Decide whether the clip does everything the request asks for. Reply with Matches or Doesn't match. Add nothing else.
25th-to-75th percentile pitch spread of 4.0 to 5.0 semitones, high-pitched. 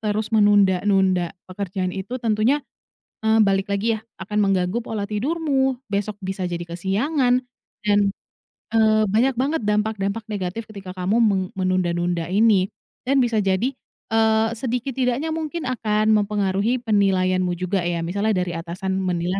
Doesn't match